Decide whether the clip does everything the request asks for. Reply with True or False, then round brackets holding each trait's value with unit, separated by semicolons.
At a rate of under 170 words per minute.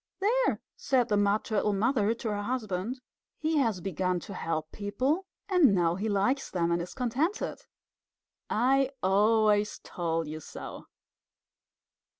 True (140 wpm)